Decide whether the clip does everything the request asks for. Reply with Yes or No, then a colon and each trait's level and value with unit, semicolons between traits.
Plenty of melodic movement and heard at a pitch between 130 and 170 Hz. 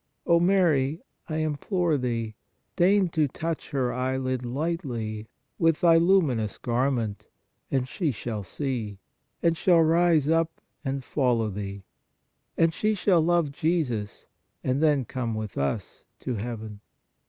Yes: wide, 5.9 semitones; medium, 140 Hz